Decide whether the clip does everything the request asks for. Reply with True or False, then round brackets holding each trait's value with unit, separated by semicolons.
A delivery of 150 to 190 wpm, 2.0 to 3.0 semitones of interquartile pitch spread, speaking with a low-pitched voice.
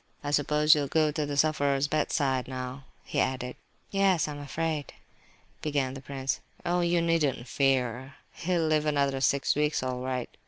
False (170 wpm; 2.6 semitones; 145 Hz)